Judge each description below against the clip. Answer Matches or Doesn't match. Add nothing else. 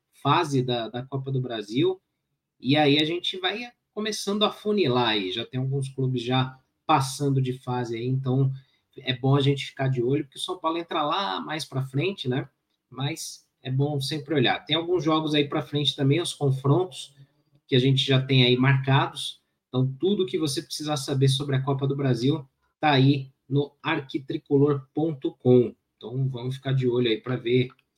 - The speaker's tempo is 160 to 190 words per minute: Matches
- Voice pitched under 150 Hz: Matches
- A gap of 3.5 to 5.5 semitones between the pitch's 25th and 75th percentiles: Doesn't match